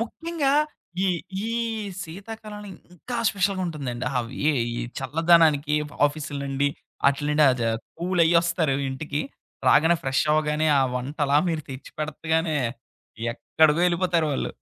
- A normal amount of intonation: Yes, average, 3.4 semitones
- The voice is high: No, medium, 155 Hz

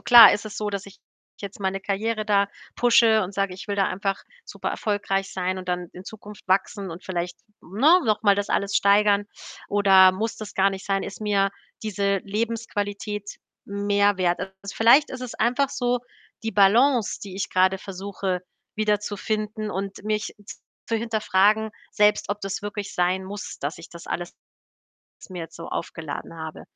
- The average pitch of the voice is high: Yes, high, 200 Hz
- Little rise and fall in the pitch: Yes, narrow, 1.9 semitones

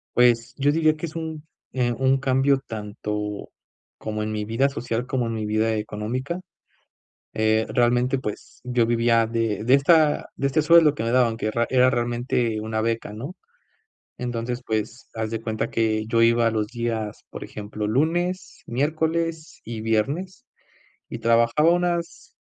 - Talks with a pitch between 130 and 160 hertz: No, low, 120 Hz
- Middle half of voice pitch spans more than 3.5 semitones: Yes, average, 3.9 semitones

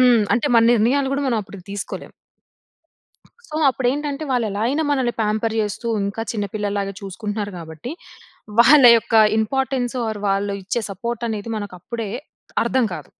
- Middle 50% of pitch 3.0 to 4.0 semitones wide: Yes, average, 3.6 semitones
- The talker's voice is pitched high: Yes, high, 225 Hz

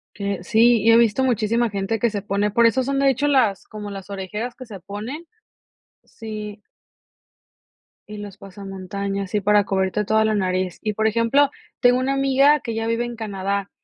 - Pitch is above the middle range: Yes, high, 215 Hz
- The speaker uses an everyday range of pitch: Yes, average, 3.1 semitones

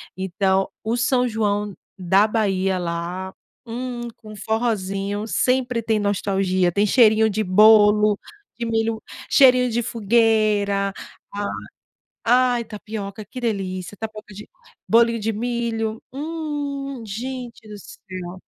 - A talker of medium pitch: No, high, 215 Hz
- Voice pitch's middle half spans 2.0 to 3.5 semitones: Yes, average, 3.0 semitones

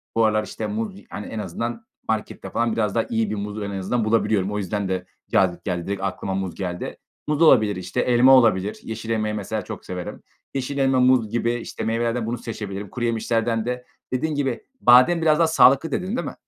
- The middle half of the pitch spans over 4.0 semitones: No, average, 3.7 semitones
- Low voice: Yes, low, 115 Hz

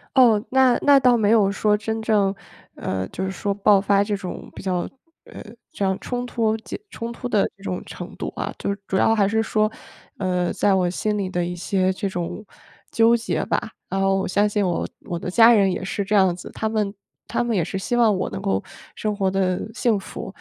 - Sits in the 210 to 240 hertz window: No, high, 200 Hz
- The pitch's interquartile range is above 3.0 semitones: No, average, 2.7 semitones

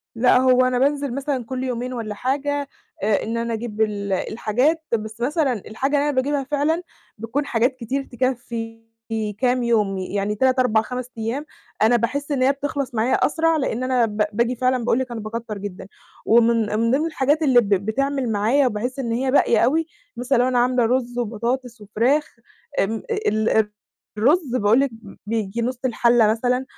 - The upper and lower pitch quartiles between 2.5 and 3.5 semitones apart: Yes, average, 3.2 semitones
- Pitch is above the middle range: Yes, high, 245 Hz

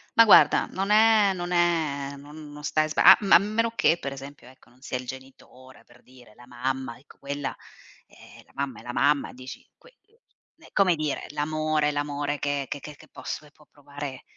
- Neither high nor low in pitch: Yes, medium, 145 Hz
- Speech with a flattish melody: No, average, 3.4 semitones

